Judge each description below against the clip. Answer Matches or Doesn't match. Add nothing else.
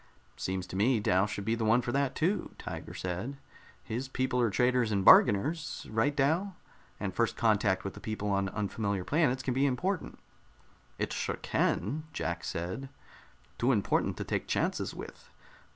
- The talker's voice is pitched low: Matches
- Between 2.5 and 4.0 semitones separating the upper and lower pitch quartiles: Doesn't match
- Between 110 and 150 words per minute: Doesn't match